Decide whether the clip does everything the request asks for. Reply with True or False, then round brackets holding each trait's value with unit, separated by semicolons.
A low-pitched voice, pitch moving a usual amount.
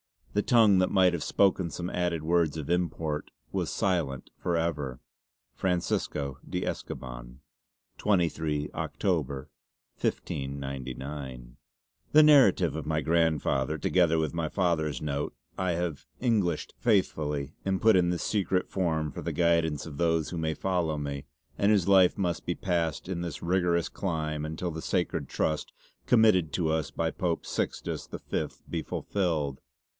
True (80 Hz; 3.3 semitones)